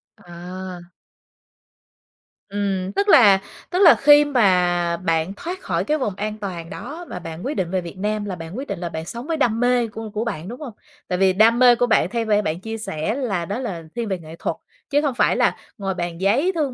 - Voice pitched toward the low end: No, high, 205 Hz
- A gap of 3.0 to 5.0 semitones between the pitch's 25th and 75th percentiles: No, wide, 5.5 semitones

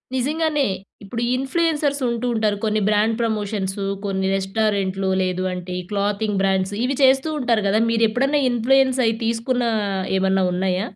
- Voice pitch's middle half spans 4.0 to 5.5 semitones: Yes, average, 4.7 semitones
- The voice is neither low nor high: No, high, 220 Hz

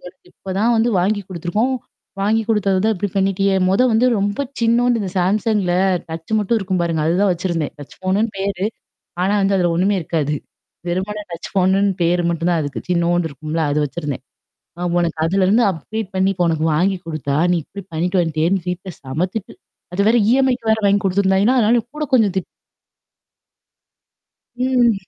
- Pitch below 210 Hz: Yes, high, 190 Hz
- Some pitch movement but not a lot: Yes, average, 3.4 semitones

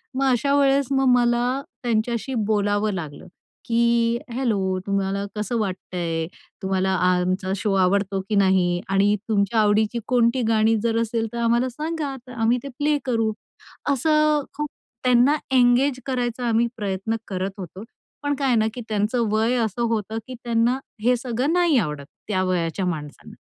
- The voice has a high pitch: Yes, high, 225 Hz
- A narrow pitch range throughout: No, average, 4.3 semitones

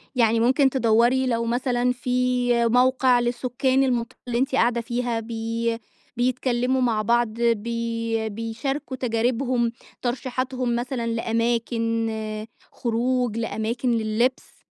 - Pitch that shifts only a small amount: Yes, narrow, 1.6 semitones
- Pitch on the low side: No, high, 240 Hz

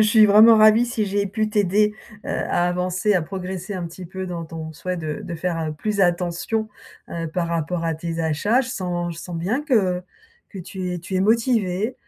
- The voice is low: No, medium, 185 Hz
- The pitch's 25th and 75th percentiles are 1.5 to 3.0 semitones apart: No, average, 3.8 semitones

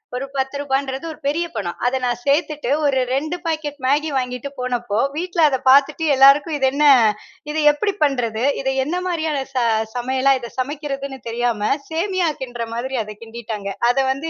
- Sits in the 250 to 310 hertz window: Yes, very high, 270 Hz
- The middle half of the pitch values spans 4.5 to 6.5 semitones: No, average, 3.5 semitones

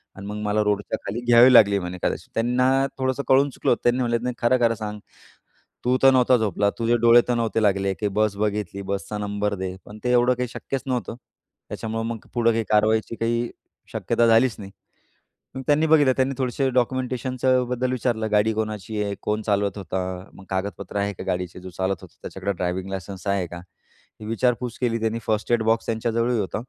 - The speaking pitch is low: Yes, low, 115 Hz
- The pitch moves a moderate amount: Yes, average, 3.3 semitones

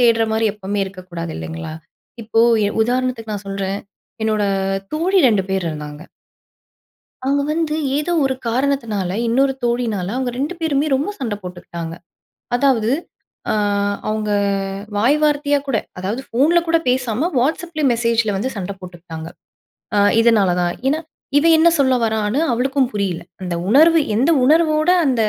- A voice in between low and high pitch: No, high, 230 Hz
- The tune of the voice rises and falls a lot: Yes, wide, 6.1 semitones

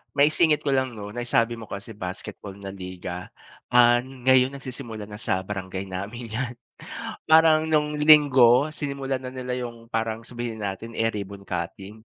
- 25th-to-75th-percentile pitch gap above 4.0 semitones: Yes, average, 4.7 semitones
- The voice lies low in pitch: Yes, low, 115 Hz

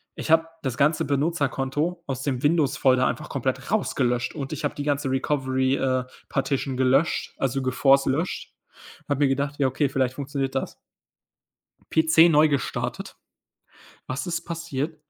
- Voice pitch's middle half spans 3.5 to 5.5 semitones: No, narrow, 2.6 semitones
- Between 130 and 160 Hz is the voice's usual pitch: Yes, medium, 140 Hz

